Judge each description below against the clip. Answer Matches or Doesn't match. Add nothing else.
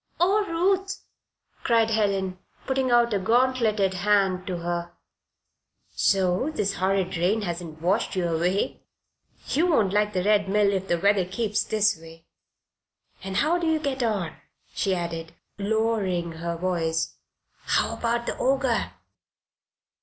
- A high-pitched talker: Matches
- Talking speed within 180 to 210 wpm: Doesn't match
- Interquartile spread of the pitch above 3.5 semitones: Matches